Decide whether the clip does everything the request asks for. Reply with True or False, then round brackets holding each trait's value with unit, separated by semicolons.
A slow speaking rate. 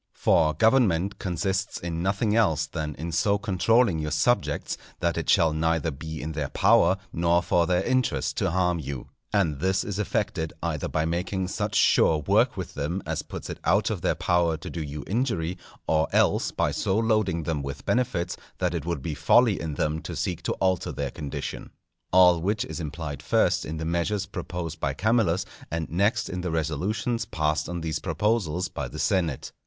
False (190 wpm)